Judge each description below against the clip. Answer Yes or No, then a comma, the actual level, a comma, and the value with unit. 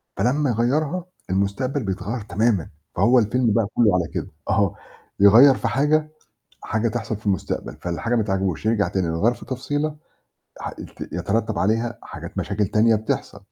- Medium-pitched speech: No, low, 110 Hz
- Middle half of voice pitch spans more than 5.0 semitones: No, average, 3.9 semitones